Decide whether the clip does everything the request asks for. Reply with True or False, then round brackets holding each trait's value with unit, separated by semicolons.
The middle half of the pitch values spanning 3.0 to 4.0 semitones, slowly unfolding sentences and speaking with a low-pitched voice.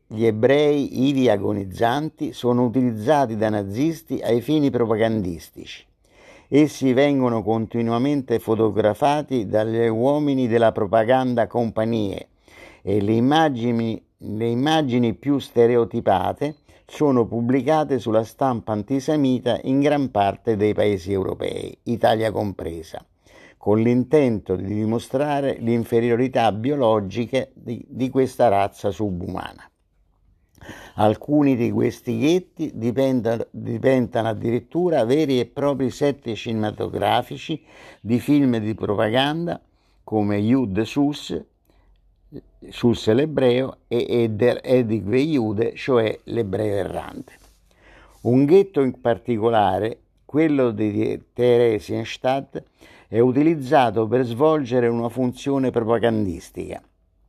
True (3.5 semitones; 95 wpm; 120 Hz)